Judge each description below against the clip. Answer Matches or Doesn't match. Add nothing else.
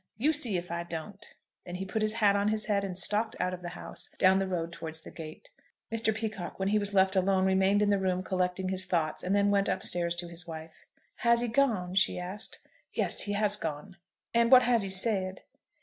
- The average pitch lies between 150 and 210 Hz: Matches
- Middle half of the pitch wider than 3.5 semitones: Doesn't match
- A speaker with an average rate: Doesn't match